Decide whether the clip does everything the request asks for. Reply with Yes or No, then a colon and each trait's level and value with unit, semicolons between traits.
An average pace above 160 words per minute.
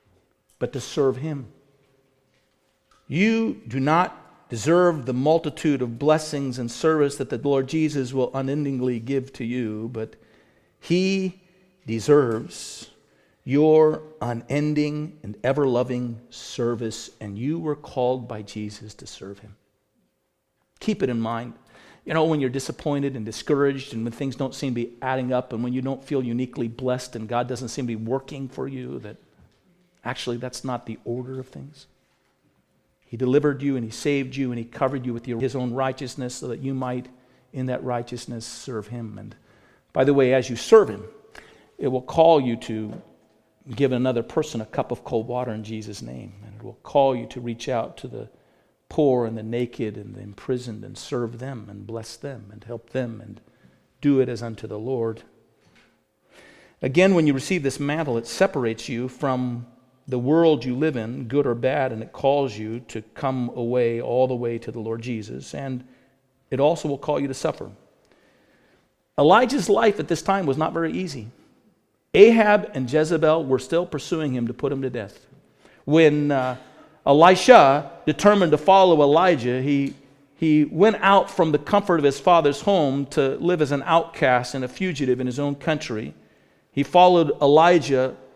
Yes: average, 175 wpm